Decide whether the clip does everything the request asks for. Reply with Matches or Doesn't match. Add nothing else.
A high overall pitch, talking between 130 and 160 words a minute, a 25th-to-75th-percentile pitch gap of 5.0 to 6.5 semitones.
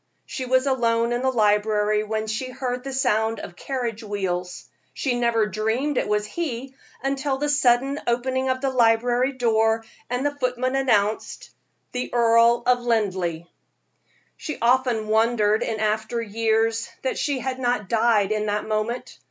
Doesn't match